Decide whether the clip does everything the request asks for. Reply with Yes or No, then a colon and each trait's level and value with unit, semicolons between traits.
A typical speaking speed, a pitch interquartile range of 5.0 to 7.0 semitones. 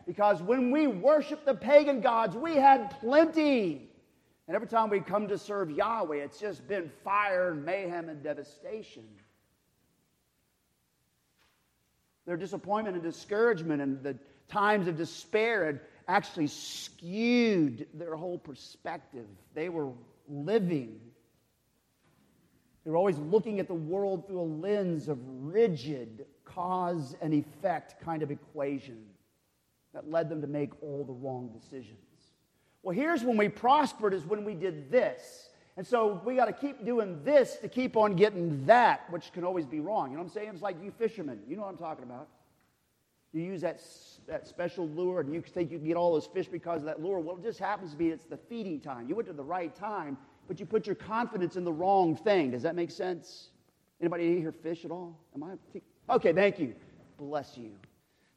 Yes: average, 180 wpm; wide, 5.5 semitones